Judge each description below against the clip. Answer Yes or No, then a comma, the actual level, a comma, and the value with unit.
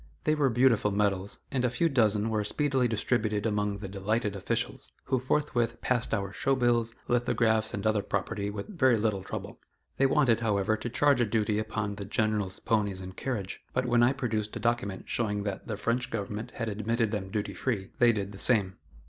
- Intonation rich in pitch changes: No, average, 2.9 semitones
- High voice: No, low, 110 Hz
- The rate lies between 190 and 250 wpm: Yes, average, 195 wpm